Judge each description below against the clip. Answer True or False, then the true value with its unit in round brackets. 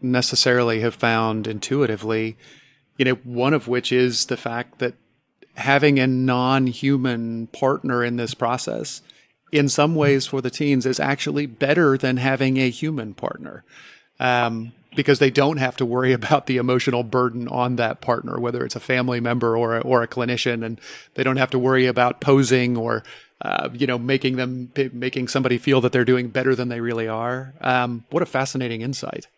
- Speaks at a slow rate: False (180 wpm)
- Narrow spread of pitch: True (1.9 semitones)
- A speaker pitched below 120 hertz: False (125 Hz)